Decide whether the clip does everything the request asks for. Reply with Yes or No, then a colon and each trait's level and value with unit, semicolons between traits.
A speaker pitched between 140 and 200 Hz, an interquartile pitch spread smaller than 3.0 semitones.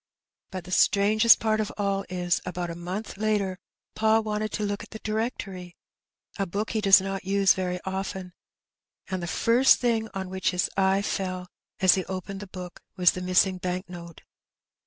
Yes: high, 190 Hz; narrow, 2.5 semitones